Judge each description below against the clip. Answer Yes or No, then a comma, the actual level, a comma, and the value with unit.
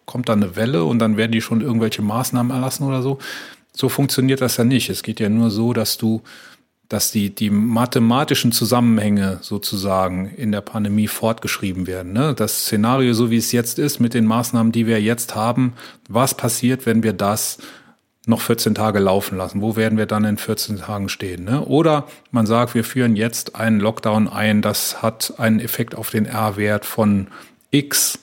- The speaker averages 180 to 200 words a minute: Yes, fast, 190 wpm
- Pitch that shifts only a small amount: Yes, narrow, 2.2 semitones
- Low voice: Yes, low, 115 Hz